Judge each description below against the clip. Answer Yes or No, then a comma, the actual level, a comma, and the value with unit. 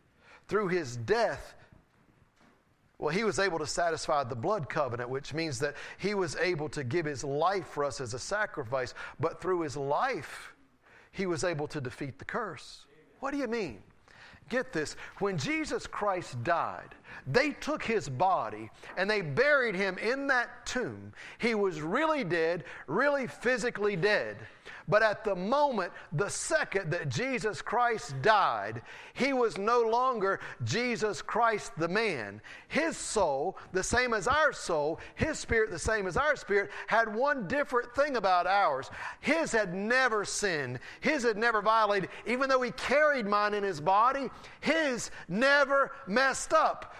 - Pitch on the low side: No, high, 205 Hz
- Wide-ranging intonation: Yes, wide, 6.9 semitones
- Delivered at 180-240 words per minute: No, average, 160 wpm